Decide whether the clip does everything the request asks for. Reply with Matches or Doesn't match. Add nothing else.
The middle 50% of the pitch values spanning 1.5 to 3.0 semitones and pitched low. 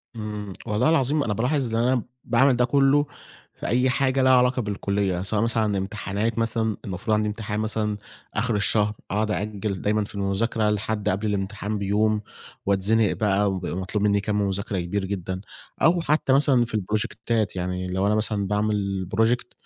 Matches